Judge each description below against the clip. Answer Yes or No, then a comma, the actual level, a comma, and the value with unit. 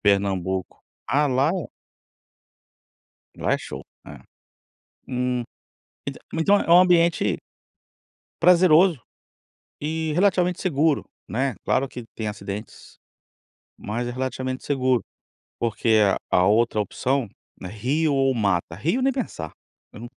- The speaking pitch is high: No, low, 130 Hz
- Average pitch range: No, wide, 7.0 semitones